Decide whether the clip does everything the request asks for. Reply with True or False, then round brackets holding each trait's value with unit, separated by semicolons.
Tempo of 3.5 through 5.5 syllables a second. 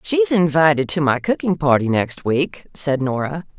True (4.5 syllables/s)